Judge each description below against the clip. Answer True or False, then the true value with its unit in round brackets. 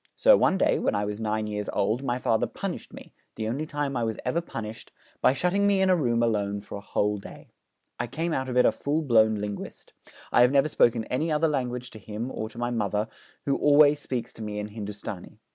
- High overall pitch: False (120 Hz)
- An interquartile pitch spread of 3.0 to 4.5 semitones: False (5.2 semitones)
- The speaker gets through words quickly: True (230 wpm)